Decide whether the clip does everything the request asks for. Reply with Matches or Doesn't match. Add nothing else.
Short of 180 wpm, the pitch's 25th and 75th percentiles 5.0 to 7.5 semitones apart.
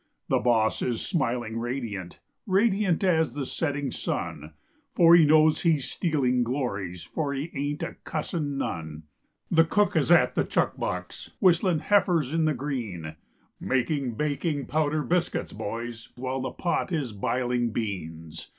Matches